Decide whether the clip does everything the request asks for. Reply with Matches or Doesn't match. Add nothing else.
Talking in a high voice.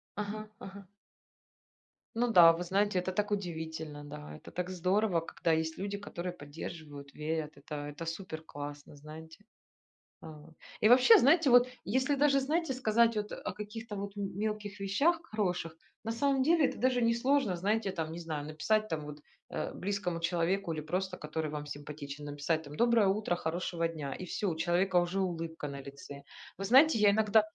Doesn't match